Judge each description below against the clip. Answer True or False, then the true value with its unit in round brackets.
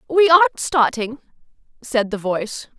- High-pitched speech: True (260 Hz)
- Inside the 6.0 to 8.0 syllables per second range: False (4.7 syllables/s)